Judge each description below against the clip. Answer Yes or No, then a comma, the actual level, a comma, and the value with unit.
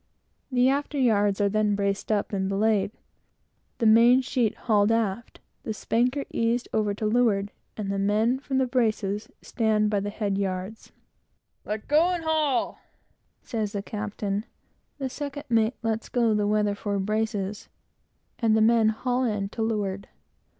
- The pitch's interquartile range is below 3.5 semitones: Yes, average, 2.9 semitones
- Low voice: No, high, 220 Hz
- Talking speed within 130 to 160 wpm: Yes, average, 155 wpm